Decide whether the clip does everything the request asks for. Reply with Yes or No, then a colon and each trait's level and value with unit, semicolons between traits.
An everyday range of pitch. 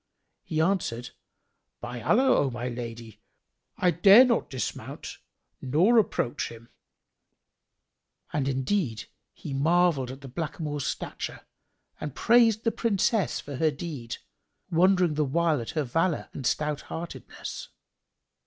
No: wide, 5.9 semitones